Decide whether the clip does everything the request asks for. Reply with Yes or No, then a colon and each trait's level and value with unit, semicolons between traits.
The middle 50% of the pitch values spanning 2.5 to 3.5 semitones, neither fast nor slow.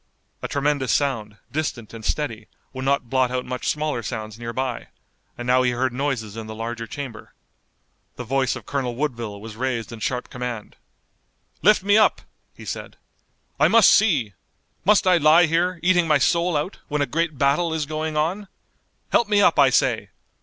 No: average, 4.9 semitones; average, 180 wpm